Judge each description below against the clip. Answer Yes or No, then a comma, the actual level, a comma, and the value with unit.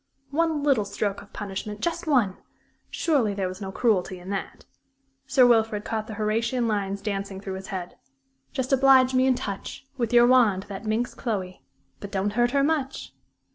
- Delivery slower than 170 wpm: No, average, 175 wpm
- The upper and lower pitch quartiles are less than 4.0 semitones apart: No, average, 4.5 semitones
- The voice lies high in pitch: Yes, high, 215 Hz